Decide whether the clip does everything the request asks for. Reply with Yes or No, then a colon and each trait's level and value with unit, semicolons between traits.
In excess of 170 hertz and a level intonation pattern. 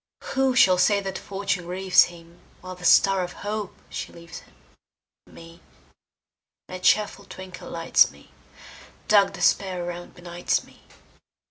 Yes: medium, 185 Hz; narrow, 2.1 semitones